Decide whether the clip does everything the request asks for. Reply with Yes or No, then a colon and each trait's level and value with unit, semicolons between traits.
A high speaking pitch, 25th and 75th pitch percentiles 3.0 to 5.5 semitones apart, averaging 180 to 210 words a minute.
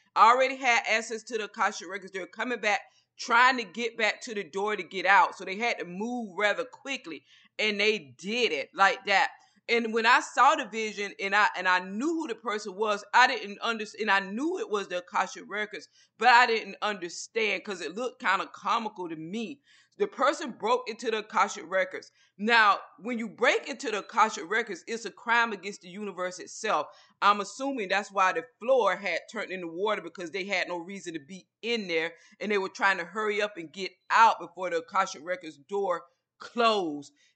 Yes: high, 210 Hz; average, 3.7 semitones; fast, 205 wpm